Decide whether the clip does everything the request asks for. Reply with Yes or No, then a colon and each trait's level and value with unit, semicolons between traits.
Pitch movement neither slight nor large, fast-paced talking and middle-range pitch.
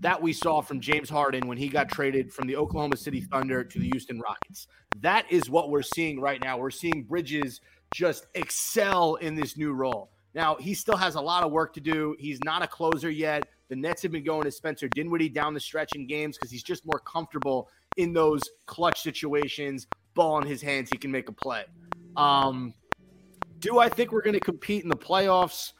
Yes: average, 3.4 semitones; fast, 215 wpm; medium, 150 Hz